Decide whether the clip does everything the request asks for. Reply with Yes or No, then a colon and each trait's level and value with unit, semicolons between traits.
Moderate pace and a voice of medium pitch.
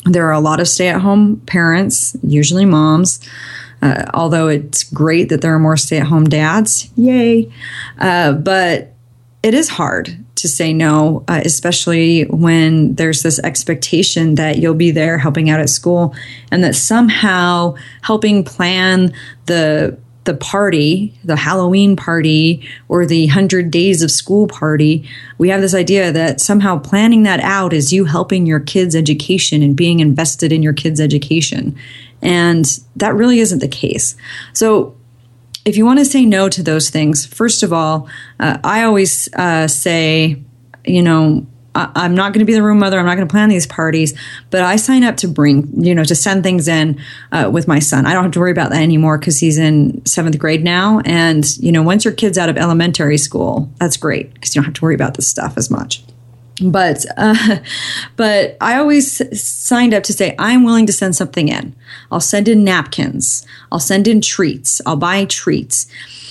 Yes: average, 185 wpm; medium, 165 Hz